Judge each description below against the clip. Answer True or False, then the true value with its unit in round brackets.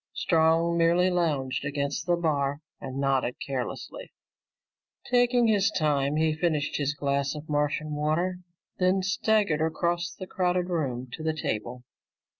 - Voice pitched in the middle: True (155 Hz)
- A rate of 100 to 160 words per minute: True (135 wpm)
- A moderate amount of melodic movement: True (4.0 semitones)